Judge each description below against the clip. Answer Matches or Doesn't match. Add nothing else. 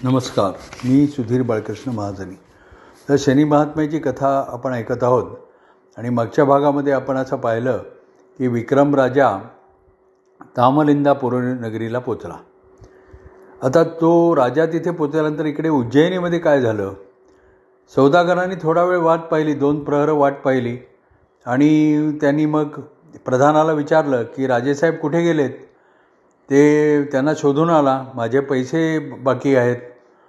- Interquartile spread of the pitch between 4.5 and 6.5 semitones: Doesn't match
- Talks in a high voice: Doesn't match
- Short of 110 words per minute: Doesn't match